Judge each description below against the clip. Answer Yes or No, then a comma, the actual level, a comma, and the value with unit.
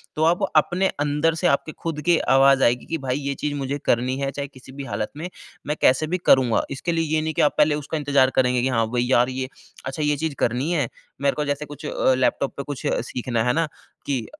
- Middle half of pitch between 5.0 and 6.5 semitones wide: No, average, 2.8 semitones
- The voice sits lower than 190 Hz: Yes, medium, 140 Hz